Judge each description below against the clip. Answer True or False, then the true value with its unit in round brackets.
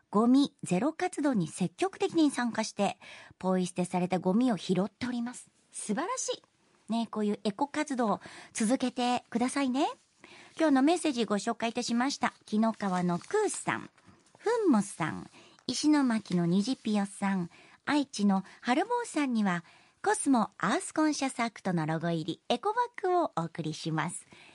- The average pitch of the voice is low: False (235 Hz)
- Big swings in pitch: True (7.5 semitones)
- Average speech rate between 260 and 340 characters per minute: True (330 characters per minute)